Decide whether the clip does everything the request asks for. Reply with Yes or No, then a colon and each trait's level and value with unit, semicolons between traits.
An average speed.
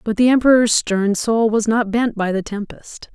No: fast, 210 wpm